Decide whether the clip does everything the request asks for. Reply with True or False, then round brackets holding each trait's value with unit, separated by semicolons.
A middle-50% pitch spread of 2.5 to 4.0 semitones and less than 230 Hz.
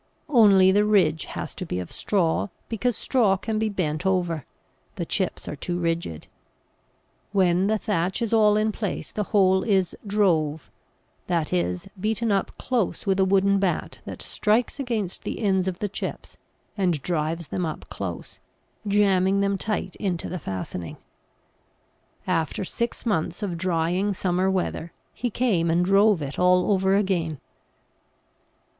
True (3.4 semitones; 190 Hz)